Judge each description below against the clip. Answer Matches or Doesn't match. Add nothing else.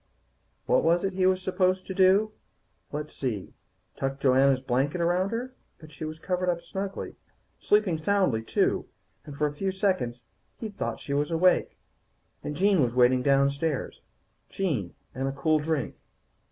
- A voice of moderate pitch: Matches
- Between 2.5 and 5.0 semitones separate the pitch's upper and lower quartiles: Doesn't match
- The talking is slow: Doesn't match